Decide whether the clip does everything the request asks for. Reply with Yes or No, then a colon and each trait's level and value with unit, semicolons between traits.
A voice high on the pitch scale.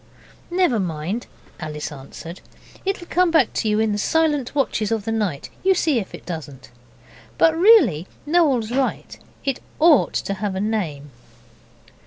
Yes: high, 220 Hz